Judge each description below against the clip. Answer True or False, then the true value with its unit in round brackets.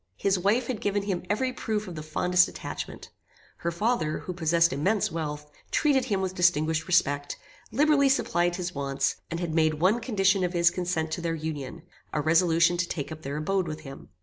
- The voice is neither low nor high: True (175 Hz)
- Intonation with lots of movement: False (3.7 semitones)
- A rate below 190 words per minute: False (195 wpm)